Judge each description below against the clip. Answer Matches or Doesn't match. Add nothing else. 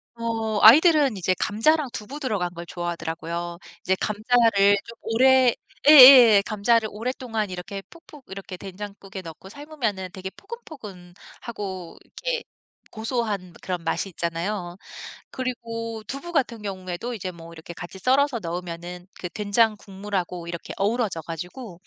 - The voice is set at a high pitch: Matches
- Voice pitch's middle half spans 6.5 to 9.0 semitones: Doesn't match